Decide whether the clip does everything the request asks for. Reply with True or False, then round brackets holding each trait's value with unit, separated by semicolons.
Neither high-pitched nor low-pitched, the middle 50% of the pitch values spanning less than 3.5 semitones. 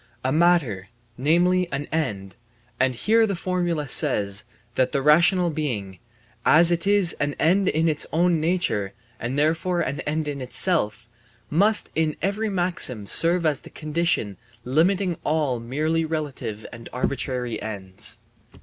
False (155 Hz; 5.6 semitones)